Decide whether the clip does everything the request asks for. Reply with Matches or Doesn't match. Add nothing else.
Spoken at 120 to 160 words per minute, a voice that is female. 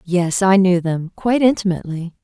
Matches